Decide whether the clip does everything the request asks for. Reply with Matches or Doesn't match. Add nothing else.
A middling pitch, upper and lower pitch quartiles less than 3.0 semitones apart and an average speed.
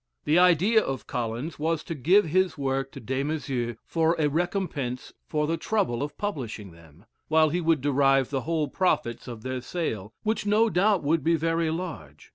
Doesn't match